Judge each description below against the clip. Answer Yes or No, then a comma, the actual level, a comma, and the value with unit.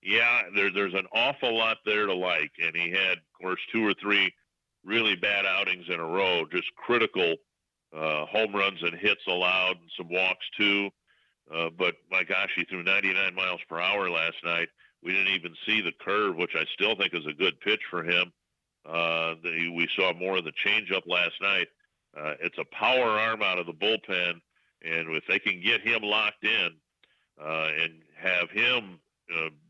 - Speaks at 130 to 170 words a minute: No, average, 190 wpm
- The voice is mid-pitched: No, very low, 95 Hz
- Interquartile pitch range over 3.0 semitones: Yes, average, 3.5 semitones